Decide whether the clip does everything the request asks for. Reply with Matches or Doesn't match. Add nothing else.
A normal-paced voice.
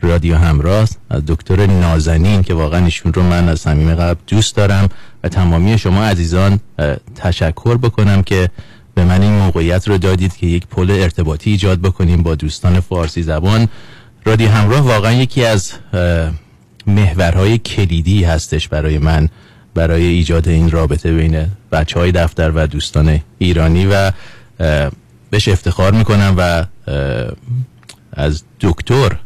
Matches